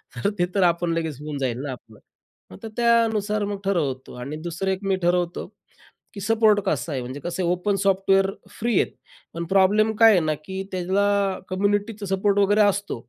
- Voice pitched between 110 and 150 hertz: No, high, 190 Hz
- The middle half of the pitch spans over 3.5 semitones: No, average, 3.2 semitones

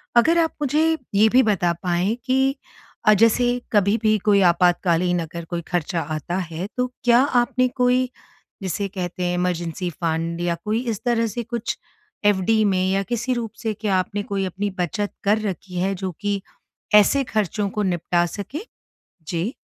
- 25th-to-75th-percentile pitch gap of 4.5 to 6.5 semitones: Yes, average, 4.9 semitones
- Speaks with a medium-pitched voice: No, high, 200 Hz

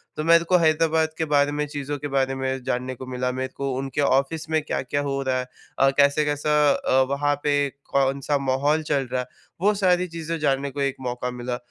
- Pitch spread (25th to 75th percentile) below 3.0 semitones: Yes, narrow, 2.4 semitones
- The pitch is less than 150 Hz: Yes, medium, 140 Hz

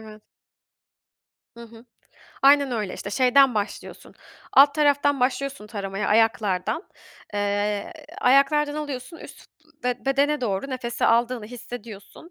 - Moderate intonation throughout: Yes, average, 4.7 semitones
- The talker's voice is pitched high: Yes, high, 245 Hz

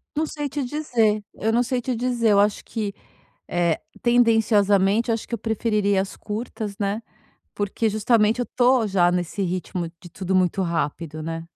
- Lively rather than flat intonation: No, average, 3.6 semitones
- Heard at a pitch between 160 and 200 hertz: No, high, 210 Hz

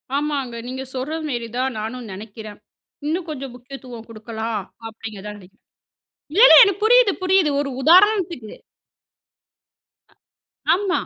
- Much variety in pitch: Yes, wide, 7.2 semitones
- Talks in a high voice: Yes, very high, 260 Hz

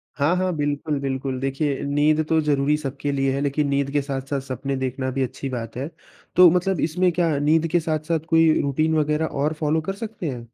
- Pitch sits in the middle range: Yes, medium, 145 Hz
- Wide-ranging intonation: No, average, 2.7 semitones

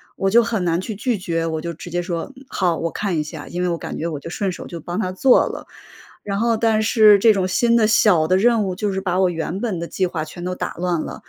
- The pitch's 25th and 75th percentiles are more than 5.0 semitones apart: No, average, 4.0 semitones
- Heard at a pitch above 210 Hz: No, medium, 185 Hz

